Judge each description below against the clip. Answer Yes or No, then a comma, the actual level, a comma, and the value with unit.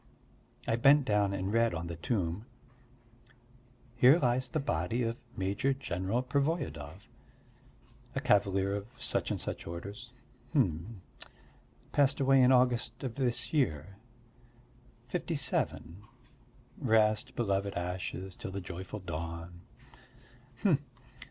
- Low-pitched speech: Yes, low, 105 Hz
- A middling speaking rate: No, slow, 115 wpm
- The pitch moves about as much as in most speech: No, wide, 5.7 semitones